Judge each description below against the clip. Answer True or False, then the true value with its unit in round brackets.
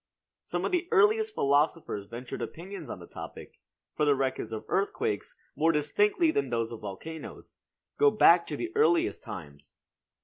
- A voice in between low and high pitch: True (160 Hz)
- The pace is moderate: True (160 wpm)